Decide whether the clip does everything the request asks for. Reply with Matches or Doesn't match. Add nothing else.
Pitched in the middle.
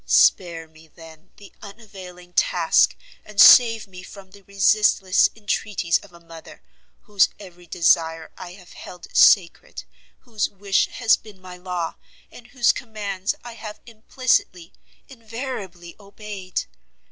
Doesn't match